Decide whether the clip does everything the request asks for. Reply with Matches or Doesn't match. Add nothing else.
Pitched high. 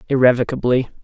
Doesn't match